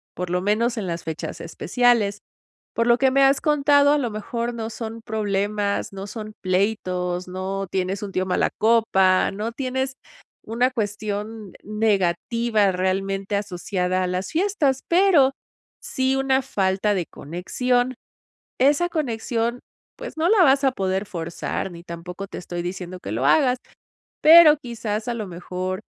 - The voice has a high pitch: Yes, high, 210 Hz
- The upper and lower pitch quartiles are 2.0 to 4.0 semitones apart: No, average, 5.1 semitones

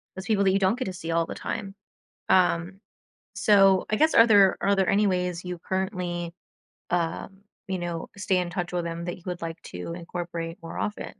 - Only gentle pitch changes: Yes, narrow, 2.3 semitones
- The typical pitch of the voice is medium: Yes, medium, 180 Hz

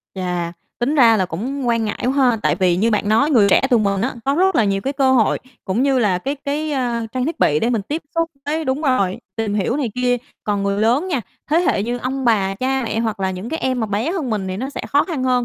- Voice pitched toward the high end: Yes, high, 240 Hz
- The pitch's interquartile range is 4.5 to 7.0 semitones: Yes, average, 5.0 semitones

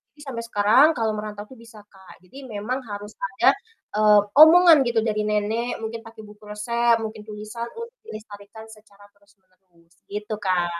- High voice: Yes, high, 215 Hz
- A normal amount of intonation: No, narrow, 2.2 semitones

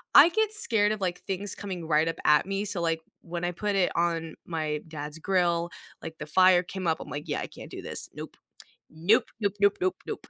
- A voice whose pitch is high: No, medium, 175 Hz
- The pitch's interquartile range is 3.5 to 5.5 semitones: Yes, average, 3.8 semitones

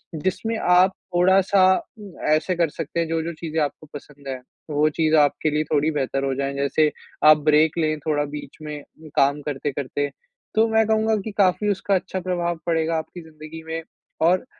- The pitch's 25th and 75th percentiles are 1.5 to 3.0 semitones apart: No, average, 3.6 semitones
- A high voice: No, medium, 160 Hz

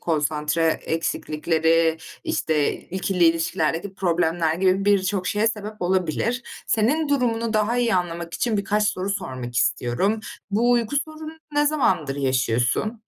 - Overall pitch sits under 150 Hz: No, medium, 185 Hz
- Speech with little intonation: No, wide, 5.4 semitones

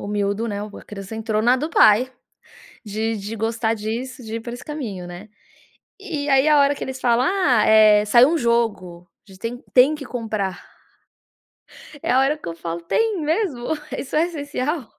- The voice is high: Yes, high, 235 Hz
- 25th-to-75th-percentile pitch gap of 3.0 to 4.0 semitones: No, average, 5.1 semitones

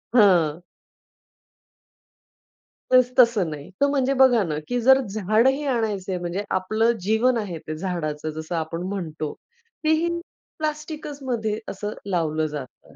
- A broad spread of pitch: Yes, wide, 6.9 semitones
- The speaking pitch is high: Yes, high, 205 Hz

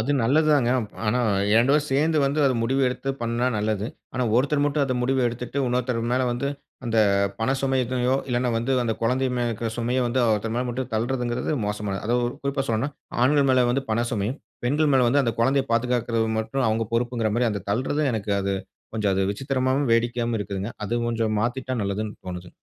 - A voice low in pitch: Yes, low, 120 Hz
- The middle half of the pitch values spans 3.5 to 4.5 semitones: No, average, 2.8 semitones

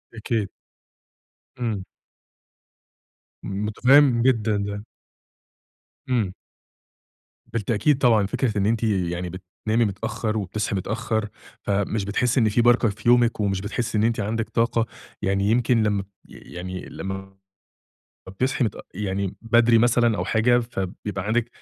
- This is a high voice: No, low, 110 Hz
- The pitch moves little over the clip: No, average, 3.0 semitones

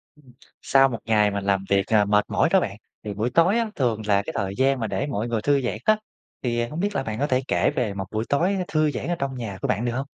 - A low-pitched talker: Yes, low, 120 Hz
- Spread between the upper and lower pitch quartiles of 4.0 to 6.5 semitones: Yes, average, 5.1 semitones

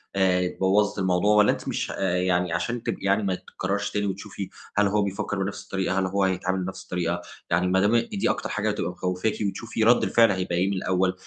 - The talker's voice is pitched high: No, very low, 95 Hz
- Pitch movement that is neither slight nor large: No, narrow, 2.1 semitones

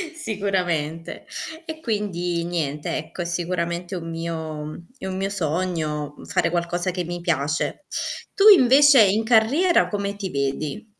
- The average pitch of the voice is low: No, medium, 175 Hz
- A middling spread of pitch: Yes, average, 3.9 semitones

